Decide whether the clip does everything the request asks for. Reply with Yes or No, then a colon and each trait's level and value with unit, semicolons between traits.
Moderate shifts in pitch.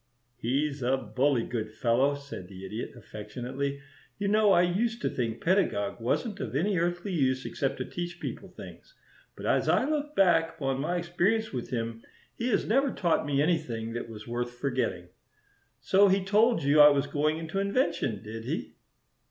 No: wide, 7.4 semitones